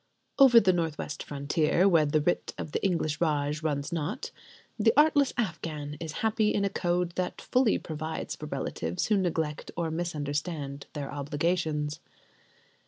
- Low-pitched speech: No, medium, 160 Hz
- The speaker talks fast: No, average, 155 wpm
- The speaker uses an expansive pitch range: No, average, 3.8 semitones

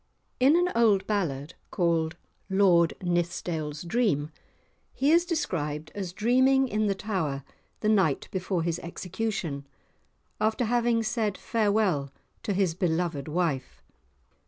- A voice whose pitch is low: No, high, 190 Hz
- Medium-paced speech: No, slow, 120 wpm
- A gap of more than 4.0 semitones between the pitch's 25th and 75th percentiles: Yes, average, 5.3 semitones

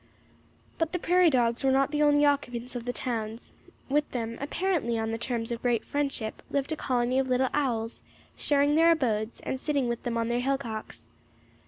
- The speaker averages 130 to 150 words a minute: No, average, 185 wpm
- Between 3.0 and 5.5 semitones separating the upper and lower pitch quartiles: Yes, average, 3.6 semitones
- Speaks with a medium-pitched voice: No, very high, 255 Hz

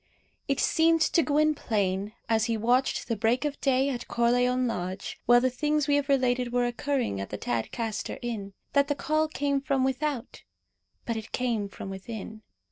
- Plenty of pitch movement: No, average, 4.1 semitones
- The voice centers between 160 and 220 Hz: No, high, 245 Hz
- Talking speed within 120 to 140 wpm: No, average, 175 wpm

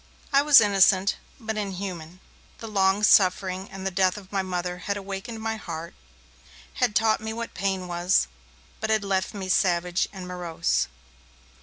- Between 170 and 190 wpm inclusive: No, average, 160 wpm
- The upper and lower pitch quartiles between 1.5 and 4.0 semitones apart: Yes, narrow, 2.5 semitones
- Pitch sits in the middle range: No, high, 195 Hz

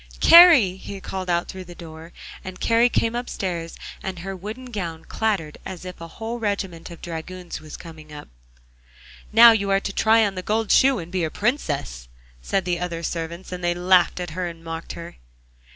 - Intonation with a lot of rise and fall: No, average, 3.7 semitones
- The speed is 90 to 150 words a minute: No, average, 195 wpm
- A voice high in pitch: No, medium, 180 Hz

